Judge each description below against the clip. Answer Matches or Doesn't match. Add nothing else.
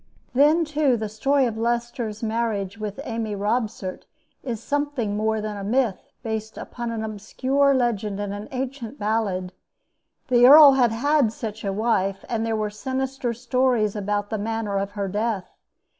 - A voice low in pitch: Doesn't match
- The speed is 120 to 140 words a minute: Doesn't match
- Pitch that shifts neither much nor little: Matches